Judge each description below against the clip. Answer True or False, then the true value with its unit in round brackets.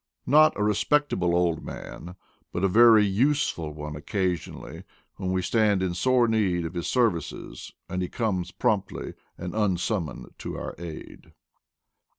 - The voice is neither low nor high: False (95 Hz)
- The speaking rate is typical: True (145 wpm)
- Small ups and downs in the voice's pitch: False (4.2 semitones)